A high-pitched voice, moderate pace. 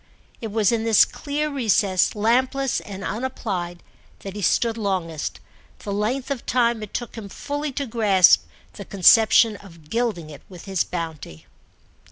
Yes: high, 215 Hz; average, 150 wpm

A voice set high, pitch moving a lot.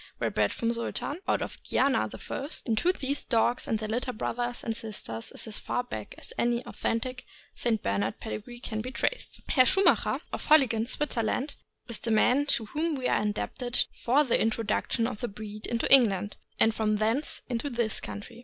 No: high, 235 Hz; average, 2.8 semitones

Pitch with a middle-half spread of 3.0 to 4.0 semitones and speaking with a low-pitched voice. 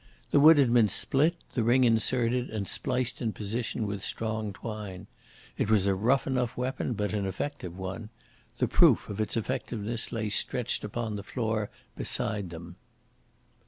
Yes: average, 3.3 semitones; low, 110 Hz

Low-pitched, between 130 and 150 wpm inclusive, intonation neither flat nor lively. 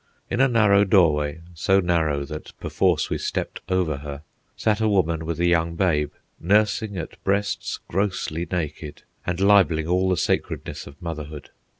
No: very low, 85 Hz; average, 160 wpm; average, 4.0 semitones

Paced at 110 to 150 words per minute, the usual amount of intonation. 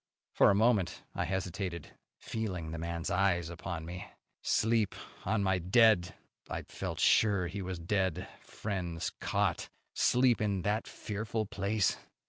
Yes: slow, 135 wpm; average, 3.5 semitones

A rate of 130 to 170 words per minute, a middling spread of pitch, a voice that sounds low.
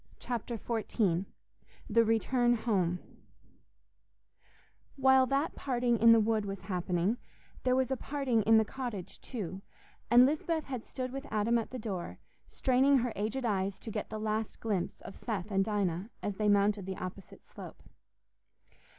No: average, 155 wpm; average, 3.9 semitones; high, 220 Hz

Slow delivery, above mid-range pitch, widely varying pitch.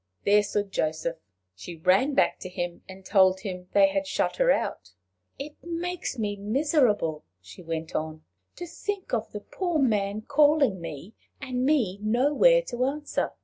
No: average, 160 wpm; high, 215 Hz; wide, 8.1 semitones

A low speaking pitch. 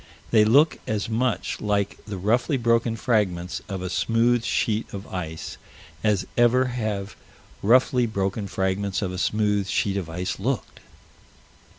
Yes: low, 105 Hz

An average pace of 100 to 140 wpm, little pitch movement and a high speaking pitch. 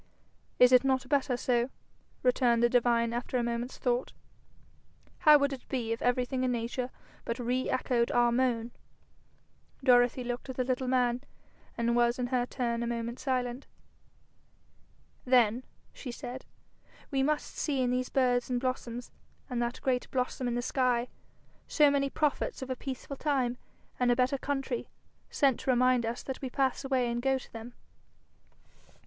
No: average, 165 wpm; narrow, 1.5 semitones; very high, 250 Hz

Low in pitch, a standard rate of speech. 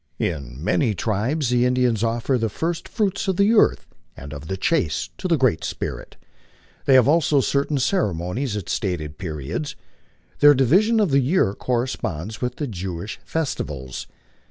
Yes: low, 120 Hz; average, 155 wpm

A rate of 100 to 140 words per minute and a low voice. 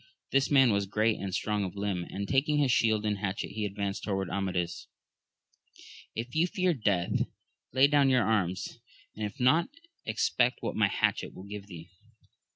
No: average, 170 wpm; low, 105 Hz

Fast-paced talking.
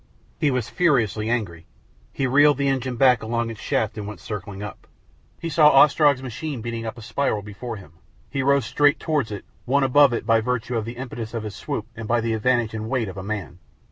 Yes: fast, 220 wpm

